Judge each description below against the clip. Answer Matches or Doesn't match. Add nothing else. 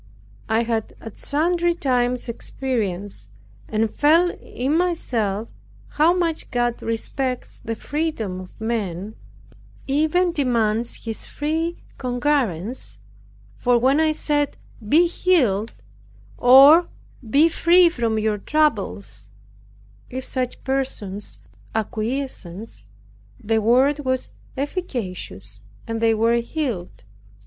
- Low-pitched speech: Doesn't match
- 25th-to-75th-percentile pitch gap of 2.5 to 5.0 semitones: Doesn't match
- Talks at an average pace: Doesn't match